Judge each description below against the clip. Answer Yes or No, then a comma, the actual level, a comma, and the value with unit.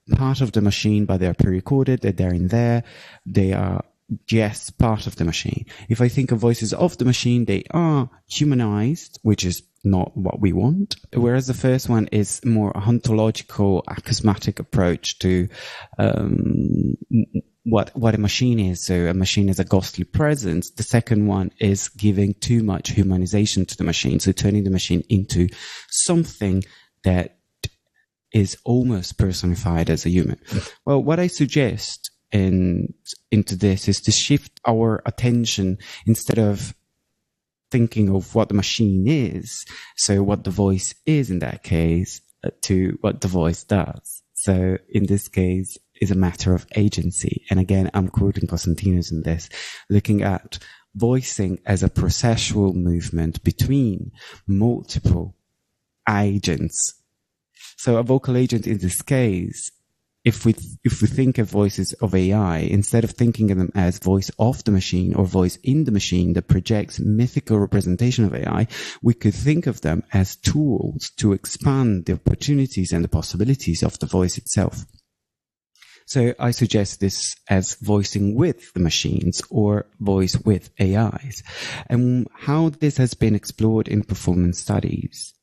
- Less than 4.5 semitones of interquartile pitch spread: Yes, average, 4.1 semitones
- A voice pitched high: No, low, 105 Hz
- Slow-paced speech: No, average, 155 wpm